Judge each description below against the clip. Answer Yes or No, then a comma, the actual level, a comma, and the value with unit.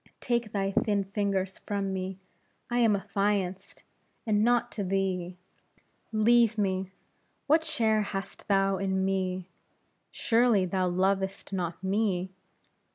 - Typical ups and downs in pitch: No, narrow, 2.1 semitones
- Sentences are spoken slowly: Yes, slow, 120 wpm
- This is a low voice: No, high, 195 Hz